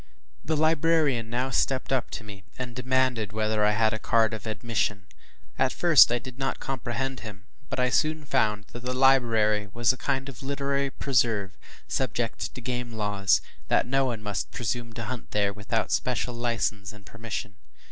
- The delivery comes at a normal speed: Yes, average, 180 wpm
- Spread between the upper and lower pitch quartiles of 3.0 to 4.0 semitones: Yes, average, 3.4 semitones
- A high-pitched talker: No, low, 120 Hz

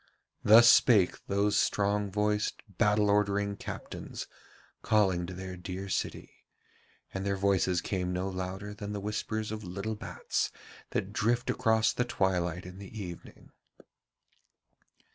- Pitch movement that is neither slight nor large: No, narrow, 2.0 semitones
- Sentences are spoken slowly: Yes, slow, 130 wpm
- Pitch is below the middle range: Yes, low, 100 Hz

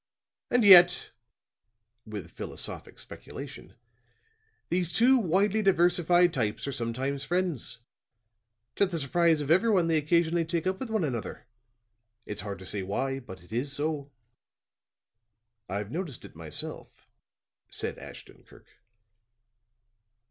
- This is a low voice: No, medium, 160 Hz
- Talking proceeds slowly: Yes, slow, 120 wpm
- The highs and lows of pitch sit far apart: Yes, wide, 5.9 semitones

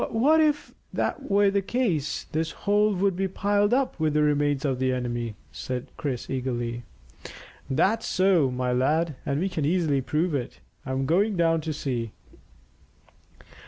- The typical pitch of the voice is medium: Yes, medium, 155 Hz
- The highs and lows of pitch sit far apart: Yes, wide, 7.0 semitones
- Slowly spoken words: No, average, 160 wpm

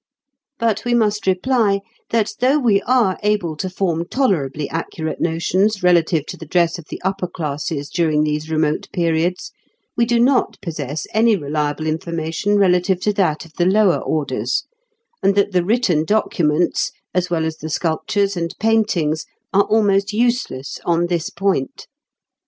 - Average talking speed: Yes, average, 155 wpm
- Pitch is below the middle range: No, medium, 180 Hz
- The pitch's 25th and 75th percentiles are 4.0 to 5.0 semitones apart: Yes, average, 4.7 semitones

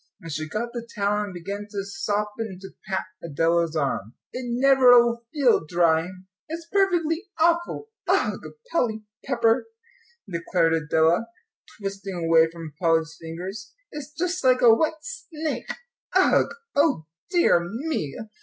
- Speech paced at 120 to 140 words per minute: Yes, slow, 135 wpm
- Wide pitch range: Yes, wide, 8.4 semitones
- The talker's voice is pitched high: Yes, high, 210 Hz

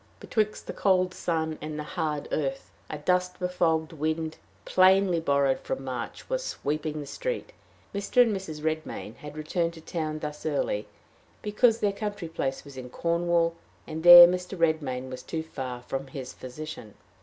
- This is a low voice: No, medium, 160 Hz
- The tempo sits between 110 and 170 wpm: Yes, average, 165 wpm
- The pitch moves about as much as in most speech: Yes, average, 3.6 semitones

